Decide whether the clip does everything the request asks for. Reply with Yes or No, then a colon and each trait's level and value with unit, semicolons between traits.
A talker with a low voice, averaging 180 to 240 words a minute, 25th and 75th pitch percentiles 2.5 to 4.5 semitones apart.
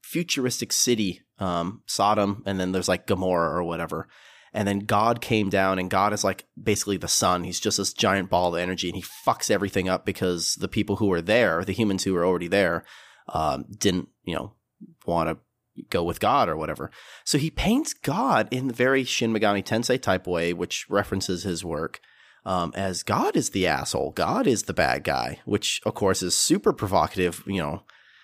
Yes: low, 100 Hz; average, 200 wpm; average, 3.1 semitones